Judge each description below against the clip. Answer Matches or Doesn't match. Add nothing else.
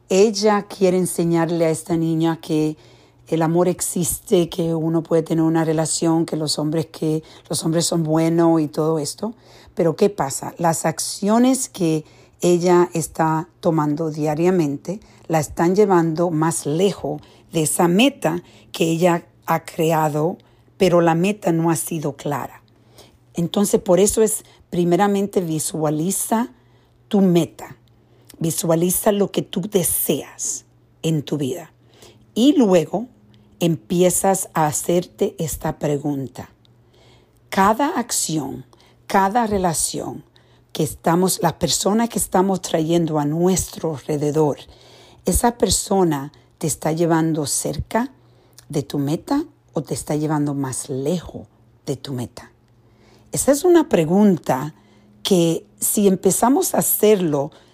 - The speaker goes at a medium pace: Doesn't match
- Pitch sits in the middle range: Matches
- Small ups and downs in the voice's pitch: Doesn't match